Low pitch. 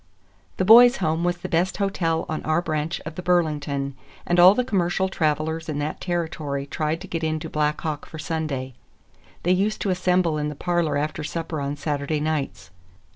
No: medium, 160 Hz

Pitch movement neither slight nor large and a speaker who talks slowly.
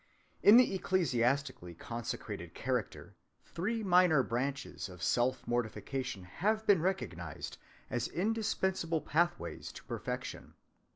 No: wide, 7.9 semitones; slow, 100 wpm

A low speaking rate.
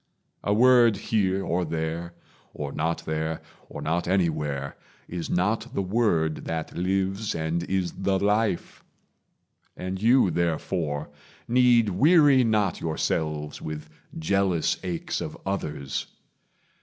Yes: slow, 120 wpm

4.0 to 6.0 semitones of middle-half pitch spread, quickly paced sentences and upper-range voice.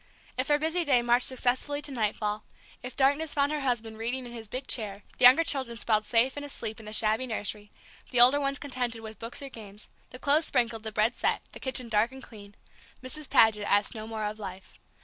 No: average, 3.6 semitones; fast, 220 wpm; high, 240 Hz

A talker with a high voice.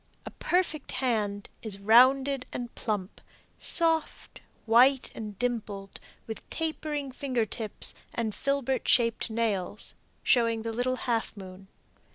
Yes: high, 235 Hz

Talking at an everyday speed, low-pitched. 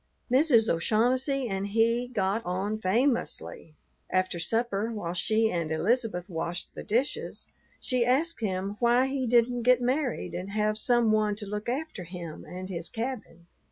No: average, 155 wpm; high, 220 Hz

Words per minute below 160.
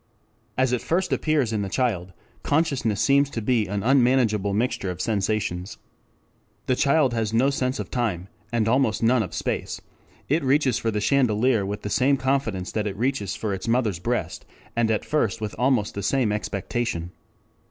No: average, 175 wpm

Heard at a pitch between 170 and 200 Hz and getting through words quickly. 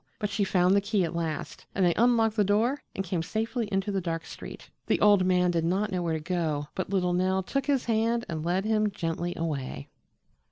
Yes: high, 190 Hz; fast, 225 wpm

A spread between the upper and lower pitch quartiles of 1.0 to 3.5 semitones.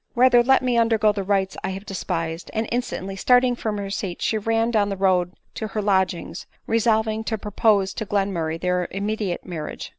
Yes: average, 2.9 semitones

